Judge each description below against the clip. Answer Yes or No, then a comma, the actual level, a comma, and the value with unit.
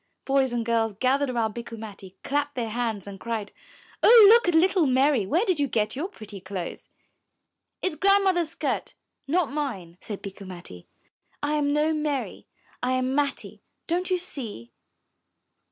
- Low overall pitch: No, very high, 260 Hz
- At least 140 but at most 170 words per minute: Yes, average, 165 wpm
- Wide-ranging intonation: Yes, wide, 6.2 semitones